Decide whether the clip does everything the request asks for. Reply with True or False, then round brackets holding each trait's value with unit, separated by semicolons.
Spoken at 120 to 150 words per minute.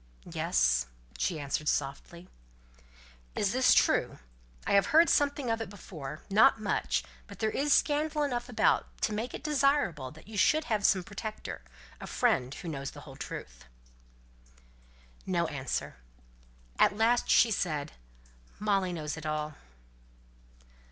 True (140 wpm)